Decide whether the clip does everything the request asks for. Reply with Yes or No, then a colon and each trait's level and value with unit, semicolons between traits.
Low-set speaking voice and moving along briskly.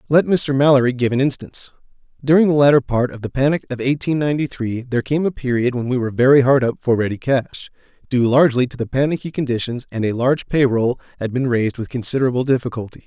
Yes: low, 130 Hz; fast, 215 wpm